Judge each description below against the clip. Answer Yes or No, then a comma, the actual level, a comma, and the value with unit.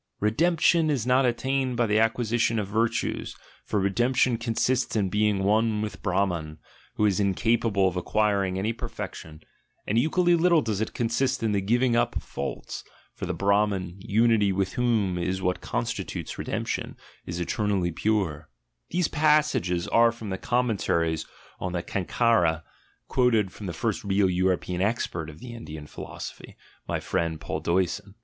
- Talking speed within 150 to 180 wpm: Yes, average, 155 wpm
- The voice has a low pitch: Yes, low, 105 Hz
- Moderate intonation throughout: Yes, average, 4.1 semitones